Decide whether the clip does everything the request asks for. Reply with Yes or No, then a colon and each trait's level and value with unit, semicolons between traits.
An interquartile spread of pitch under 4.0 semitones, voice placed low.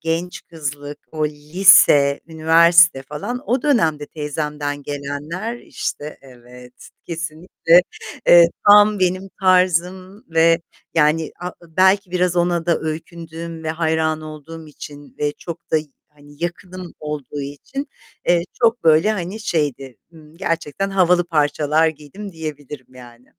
No: average, 3.3 semitones; medium, 160 Hz